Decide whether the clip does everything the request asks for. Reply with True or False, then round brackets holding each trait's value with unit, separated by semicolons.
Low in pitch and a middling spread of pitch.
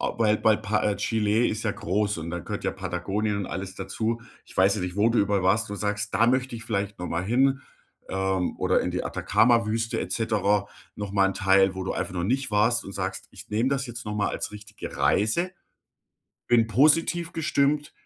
True (105 Hz; 3.1 semitones)